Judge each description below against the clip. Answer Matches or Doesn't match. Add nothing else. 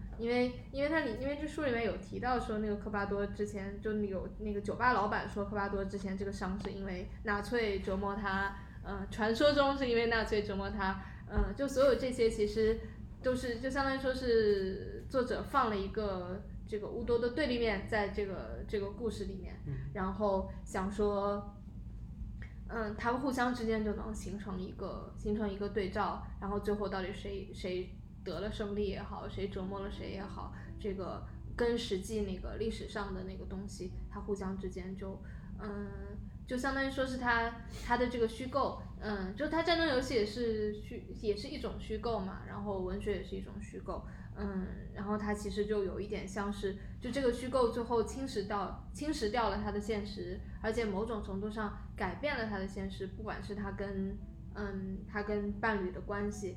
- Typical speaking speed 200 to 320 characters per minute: Matches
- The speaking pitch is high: Matches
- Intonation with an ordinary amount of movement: Matches